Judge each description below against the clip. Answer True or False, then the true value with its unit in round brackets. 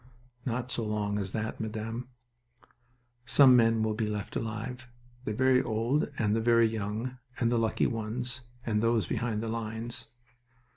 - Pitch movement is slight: True (1.9 semitones)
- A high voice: False (115 Hz)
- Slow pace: False (155 wpm)